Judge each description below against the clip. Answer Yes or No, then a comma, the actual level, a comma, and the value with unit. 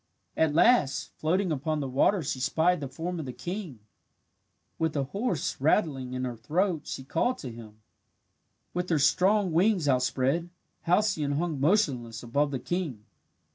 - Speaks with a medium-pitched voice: Yes, medium, 155 Hz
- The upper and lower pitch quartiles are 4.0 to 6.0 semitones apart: Yes, average, 5.3 semitones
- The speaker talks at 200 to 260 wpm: No, average, 155 wpm